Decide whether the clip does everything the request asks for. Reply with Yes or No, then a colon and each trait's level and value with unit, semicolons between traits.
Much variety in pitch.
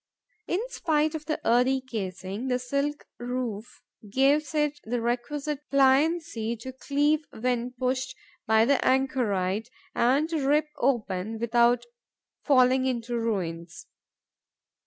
No: average, 3.8 semitones